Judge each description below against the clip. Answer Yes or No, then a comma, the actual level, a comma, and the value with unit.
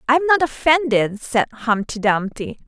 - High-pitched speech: Yes, very high, 250 Hz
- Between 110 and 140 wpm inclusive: Yes, slow, 135 wpm